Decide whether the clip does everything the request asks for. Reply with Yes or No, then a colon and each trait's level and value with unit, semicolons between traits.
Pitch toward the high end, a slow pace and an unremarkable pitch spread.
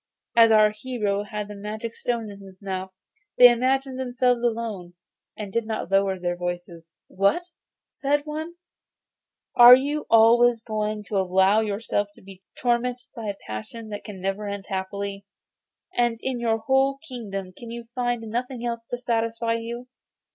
No: high, 225 Hz; average, 160 wpm; average, 3.4 semitones